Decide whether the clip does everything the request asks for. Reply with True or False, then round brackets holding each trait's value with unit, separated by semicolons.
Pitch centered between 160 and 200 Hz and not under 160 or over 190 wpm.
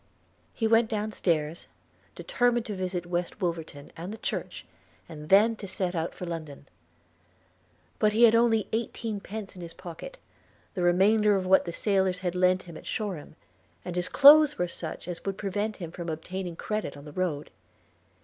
True (185 Hz; 175 wpm)